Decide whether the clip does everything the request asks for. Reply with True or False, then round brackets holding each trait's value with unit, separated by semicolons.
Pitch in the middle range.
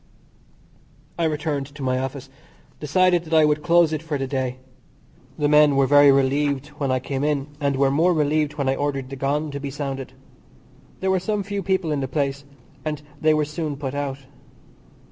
True (145 Hz)